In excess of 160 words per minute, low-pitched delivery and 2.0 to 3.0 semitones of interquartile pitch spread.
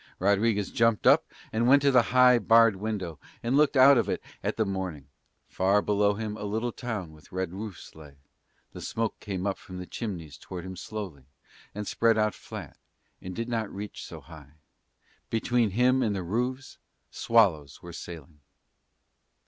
No: average, 175 wpm; low, 105 Hz; average, 4.0 semitones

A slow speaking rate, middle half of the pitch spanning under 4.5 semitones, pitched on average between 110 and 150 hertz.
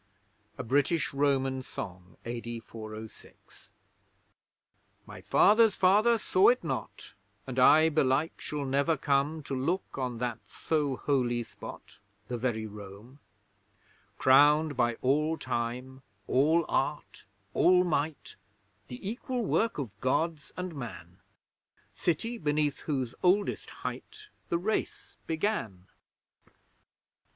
No: slow, 110 wpm; average, 5.0 semitones; medium, 140 Hz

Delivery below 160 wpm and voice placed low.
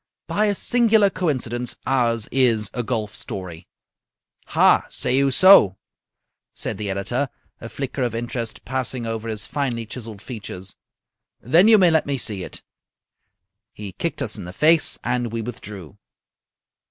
Yes: average, 150 wpm; low, 120 Hz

